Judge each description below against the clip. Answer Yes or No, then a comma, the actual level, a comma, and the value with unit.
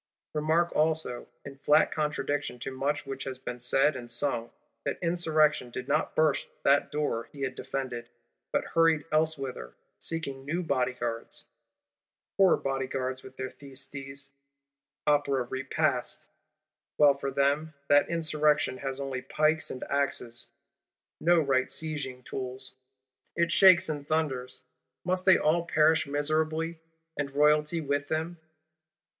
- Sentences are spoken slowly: Yes, slow, 130 wpm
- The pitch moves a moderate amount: Yes, average, 3.0 semitones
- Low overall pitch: No, medium, 145 Hz